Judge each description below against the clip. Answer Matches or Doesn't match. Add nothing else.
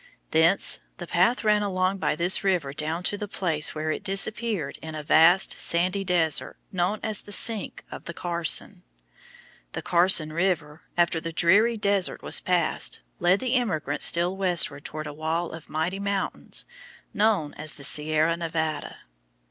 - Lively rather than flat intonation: Doesn't match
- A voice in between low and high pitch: Matches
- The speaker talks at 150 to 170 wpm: Matches